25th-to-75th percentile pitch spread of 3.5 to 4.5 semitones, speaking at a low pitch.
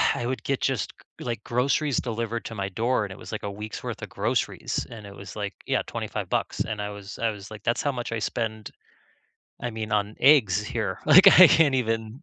No: average, 2.8 semitones; low, 110 Hz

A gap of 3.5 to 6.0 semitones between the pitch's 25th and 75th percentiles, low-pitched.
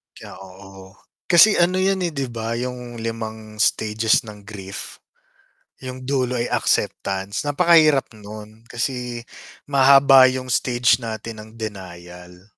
Yes: average, 3.8 semitones; low, 115 Hz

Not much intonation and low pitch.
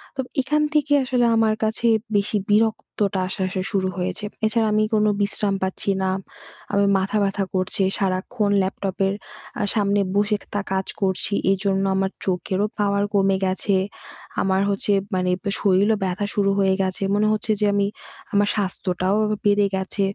No: narrow, 1.7 semitones; high, 200 Hz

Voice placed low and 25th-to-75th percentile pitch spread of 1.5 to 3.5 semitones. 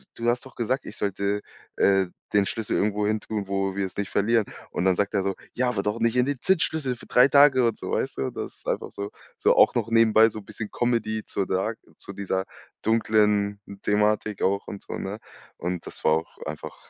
Yes: low, 105 Hz; average, 2.7 semitones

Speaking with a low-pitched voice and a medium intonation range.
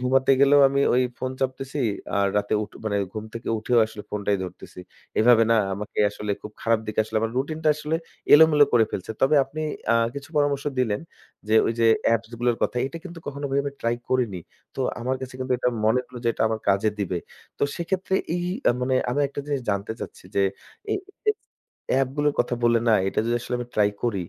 Yes: low, 125 Hz; average, 4.2 semitones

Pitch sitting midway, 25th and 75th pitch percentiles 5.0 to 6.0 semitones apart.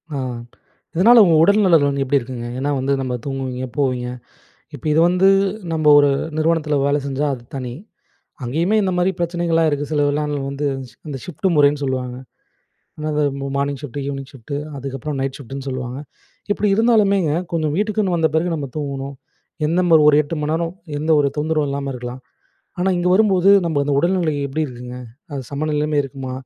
No: medium, 145 Hz; average, 3.5 semitones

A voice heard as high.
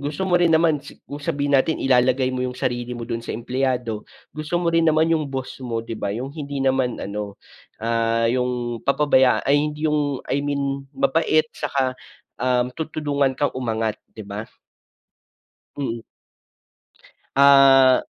No: low, 135 Hz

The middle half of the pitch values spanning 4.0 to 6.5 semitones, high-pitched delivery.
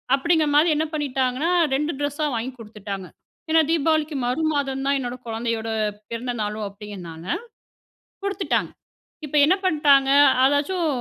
Yes: average, 5.1 semitones; very high, 275 Hz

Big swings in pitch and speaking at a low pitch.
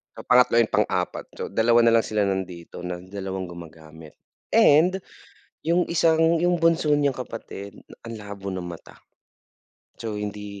Yes: wide, 7.7 semitones; low, 105 Hz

